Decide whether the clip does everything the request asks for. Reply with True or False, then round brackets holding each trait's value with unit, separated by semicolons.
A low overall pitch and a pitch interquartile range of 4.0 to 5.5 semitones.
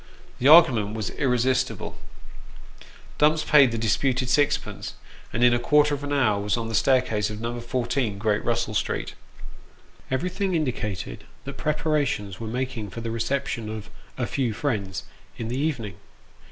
True (120 Hz; 4.4 semitones)